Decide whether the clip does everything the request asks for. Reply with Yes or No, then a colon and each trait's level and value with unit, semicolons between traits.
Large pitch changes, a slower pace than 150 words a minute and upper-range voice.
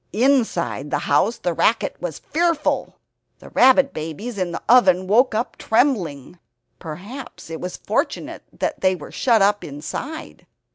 Yes: wide, 6.6 semitones; average, 140 wpm; high, 205 Hz